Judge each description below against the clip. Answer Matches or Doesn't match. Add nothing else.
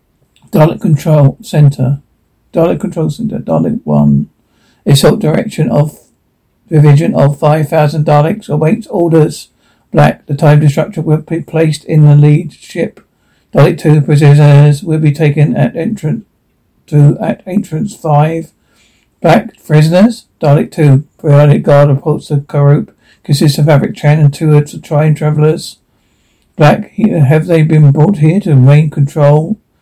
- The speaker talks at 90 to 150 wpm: Matches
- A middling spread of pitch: Doesn't match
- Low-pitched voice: Doesn't match